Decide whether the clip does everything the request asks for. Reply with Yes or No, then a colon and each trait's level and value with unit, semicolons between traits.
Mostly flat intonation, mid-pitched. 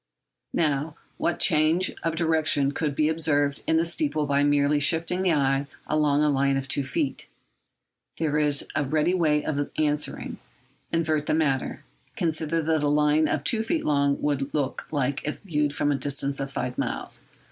Yes: narrow, 2.0 semitones; medium, 150 Hz